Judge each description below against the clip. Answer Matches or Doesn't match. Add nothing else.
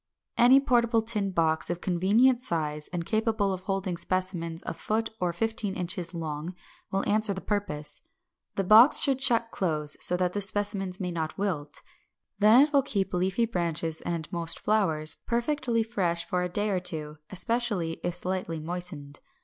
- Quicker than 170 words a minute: Doesn't match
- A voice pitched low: Doesn't match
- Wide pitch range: Doesn't match